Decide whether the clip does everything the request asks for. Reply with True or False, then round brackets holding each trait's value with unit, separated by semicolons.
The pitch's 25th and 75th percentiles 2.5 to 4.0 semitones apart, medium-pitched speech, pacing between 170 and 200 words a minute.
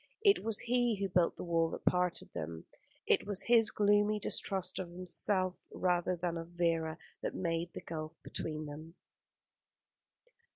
False (3.6 semitones; 180 Hz; 155 wpm)